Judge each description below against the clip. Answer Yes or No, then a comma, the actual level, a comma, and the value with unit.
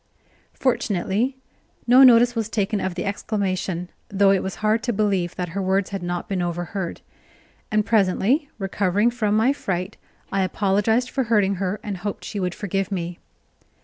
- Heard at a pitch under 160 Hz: No, high, 200 Hz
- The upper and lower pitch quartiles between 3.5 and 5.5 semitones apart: No, average, 3.0 semitones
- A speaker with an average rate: Yes, average, 165 wpm